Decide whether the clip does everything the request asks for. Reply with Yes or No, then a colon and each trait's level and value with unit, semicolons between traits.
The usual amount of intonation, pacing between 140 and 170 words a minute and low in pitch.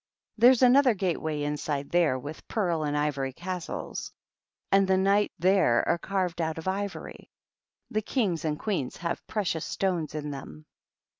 No: average, 4.7 semitones; average, 155 wpm; medium, 175 Hz